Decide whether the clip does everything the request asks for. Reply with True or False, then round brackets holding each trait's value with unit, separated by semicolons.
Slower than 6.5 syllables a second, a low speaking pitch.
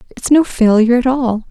False (6.0 syllables/s; 245 Hz)